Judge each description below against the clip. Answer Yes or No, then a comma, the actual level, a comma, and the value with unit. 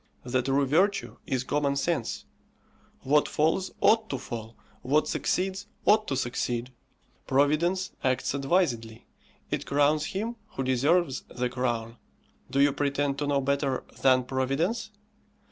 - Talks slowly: Yes, slow, 130 wpm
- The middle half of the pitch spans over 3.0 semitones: Yes, average, 4.1 semitones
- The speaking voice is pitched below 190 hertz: Yes, medium, 140 Hz